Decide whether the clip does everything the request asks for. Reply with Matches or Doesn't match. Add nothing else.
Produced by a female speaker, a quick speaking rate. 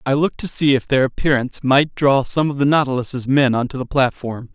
Doesn't match